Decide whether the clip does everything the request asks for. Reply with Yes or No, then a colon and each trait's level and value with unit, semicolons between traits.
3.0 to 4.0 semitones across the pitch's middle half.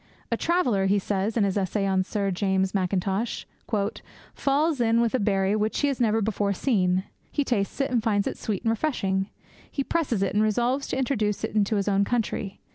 Yes: average, 3.6 semitones